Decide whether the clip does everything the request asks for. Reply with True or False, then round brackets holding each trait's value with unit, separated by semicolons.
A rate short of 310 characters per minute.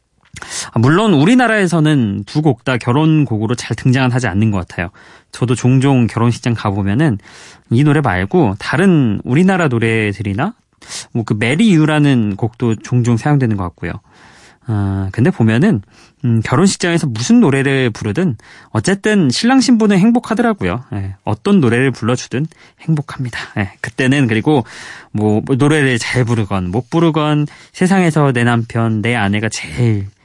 False (315 characters per minute)